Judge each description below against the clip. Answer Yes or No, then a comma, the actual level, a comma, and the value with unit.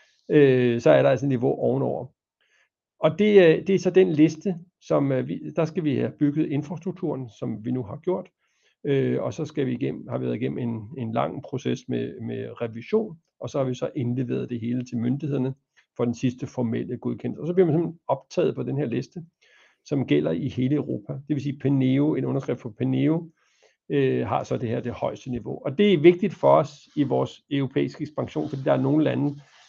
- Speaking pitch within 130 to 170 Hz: Yes, medium, 140 Hz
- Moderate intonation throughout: Yes, average, 4.3 semitones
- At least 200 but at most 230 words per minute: Yes, average, 210 wpm